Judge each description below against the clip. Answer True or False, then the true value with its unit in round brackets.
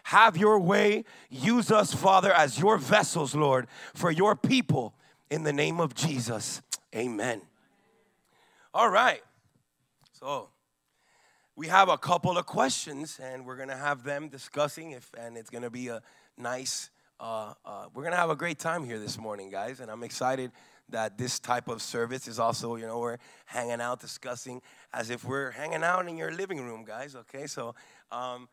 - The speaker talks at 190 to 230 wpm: False (180 wpm)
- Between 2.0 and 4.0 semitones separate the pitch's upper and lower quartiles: False (5.4 semitones)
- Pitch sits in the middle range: False (130 Hz)